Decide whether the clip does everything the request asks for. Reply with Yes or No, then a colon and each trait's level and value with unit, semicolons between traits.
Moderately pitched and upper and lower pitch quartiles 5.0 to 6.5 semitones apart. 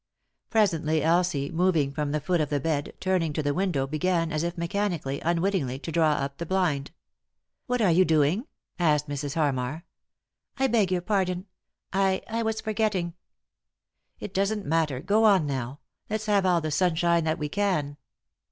No: medium, 170 Hz; average, 4.3 semitones